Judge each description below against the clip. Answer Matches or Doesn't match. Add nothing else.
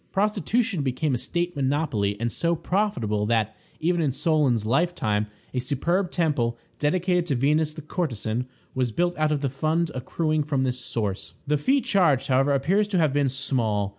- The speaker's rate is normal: Matches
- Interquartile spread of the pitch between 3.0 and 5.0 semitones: Doesn't match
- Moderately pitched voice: Matches